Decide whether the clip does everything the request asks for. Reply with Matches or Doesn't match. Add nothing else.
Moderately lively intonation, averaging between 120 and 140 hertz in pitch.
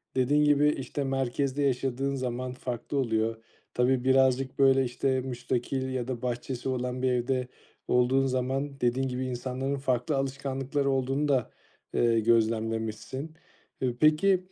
Doesn't match